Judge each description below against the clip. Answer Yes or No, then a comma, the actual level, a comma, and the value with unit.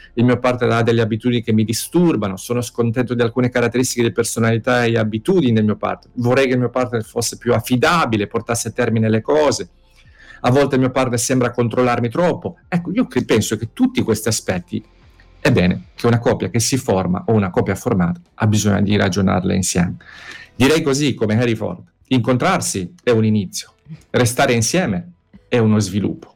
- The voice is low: Yes, low, 115 Hz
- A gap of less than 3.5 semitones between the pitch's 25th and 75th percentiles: Yes, average, 2.9 semitones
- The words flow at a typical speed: No, fast, 185 wpm